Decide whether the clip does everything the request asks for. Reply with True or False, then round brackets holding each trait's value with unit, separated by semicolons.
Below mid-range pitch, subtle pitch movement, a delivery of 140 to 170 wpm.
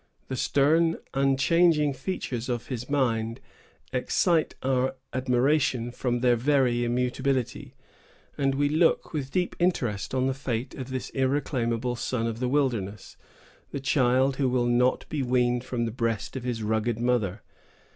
True (125 Hz; 2.3 semitones; 145 wpm)